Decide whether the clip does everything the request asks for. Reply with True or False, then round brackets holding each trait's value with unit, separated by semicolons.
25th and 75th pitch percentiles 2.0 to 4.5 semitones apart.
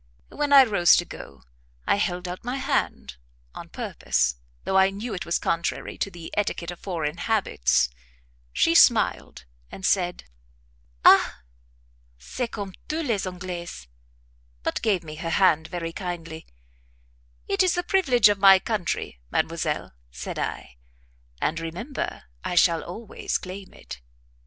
True (3.9 semitones)